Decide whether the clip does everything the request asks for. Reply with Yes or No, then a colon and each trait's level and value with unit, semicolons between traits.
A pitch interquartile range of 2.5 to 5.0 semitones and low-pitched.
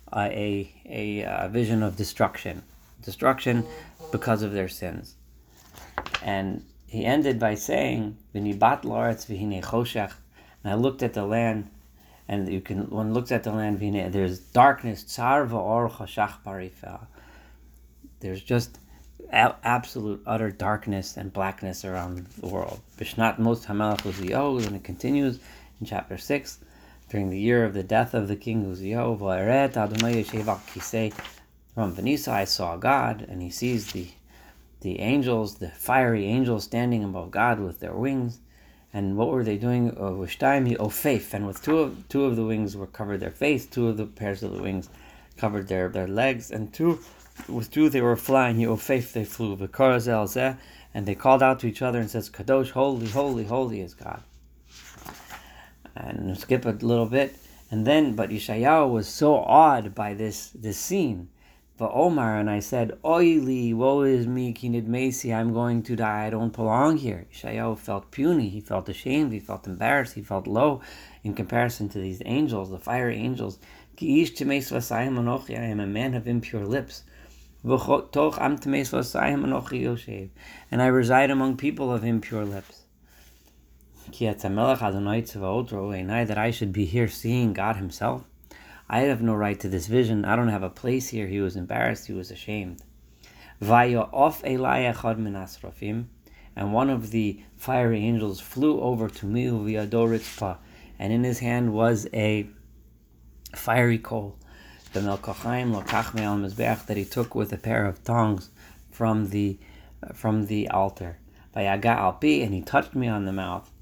Yes: average, 3.6 semitones; low, 110 Hz